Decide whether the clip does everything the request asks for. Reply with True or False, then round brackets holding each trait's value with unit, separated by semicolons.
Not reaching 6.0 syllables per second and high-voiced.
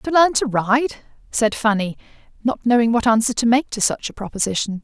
True (5.4 syllables/s; 230 Hz)